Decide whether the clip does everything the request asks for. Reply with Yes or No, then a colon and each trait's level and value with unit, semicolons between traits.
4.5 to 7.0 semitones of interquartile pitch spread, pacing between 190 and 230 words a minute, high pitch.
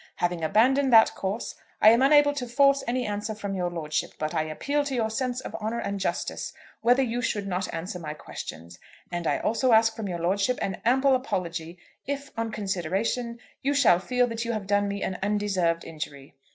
Yes: wide, 5.6 semitones; average, 200 wpm; high, 215 Hz